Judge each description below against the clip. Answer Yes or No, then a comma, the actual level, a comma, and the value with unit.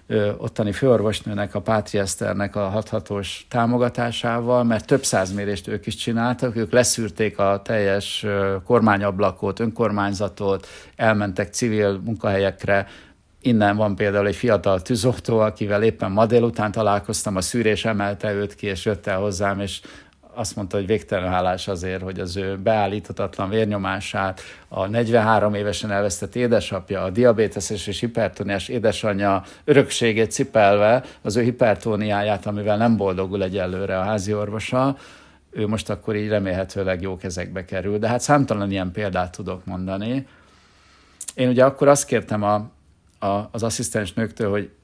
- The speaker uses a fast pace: No, average, 140 wpm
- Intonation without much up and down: Yes, narrow, 2.3 semitones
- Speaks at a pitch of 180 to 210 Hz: No, low, 105 Hz